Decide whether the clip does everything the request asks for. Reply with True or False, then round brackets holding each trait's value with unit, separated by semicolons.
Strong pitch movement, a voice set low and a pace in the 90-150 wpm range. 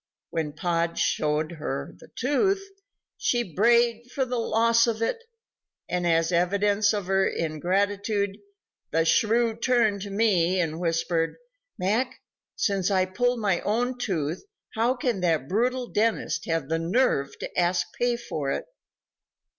False (5.7 semitones; 200 Hz; 140 wpm)